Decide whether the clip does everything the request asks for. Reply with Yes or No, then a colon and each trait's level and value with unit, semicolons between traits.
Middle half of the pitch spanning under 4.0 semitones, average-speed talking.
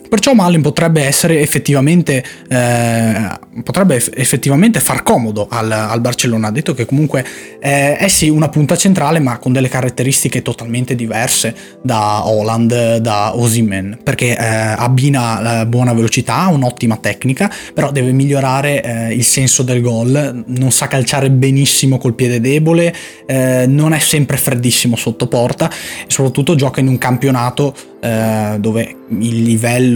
Yes: average, 3.5 semitones; average, 150 wpm